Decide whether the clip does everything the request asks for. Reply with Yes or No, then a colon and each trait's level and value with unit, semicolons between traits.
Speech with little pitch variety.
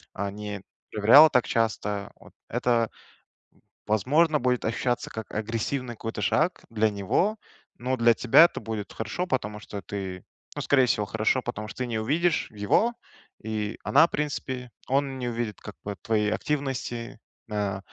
No: average, 3.8 semitones